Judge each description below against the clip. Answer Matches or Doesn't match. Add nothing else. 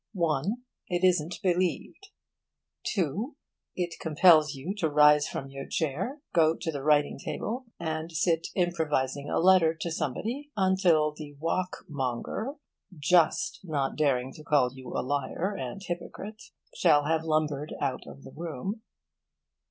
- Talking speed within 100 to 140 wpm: Matches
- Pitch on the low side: Doesn't match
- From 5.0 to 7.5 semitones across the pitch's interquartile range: Doesn't match